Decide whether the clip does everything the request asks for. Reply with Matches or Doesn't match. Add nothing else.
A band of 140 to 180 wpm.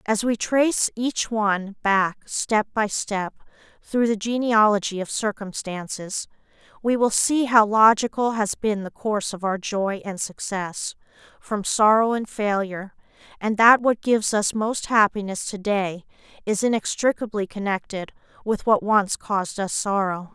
Matches